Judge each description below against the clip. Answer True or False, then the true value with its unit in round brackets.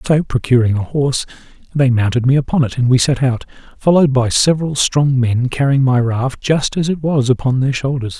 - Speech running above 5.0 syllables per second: True (5.5 syllables/s)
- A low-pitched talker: True (130 Hz)